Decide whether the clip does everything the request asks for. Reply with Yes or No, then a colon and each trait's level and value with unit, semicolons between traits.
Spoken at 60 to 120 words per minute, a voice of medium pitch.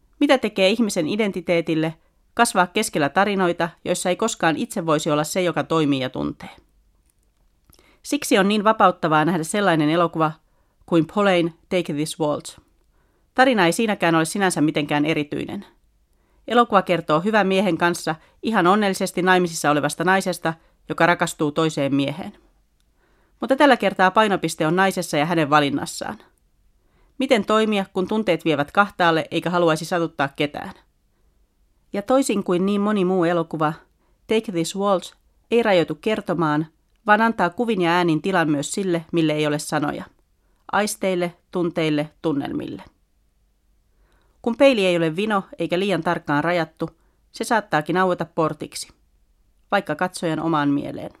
No: average, 135 wpm; medium, 175 Hz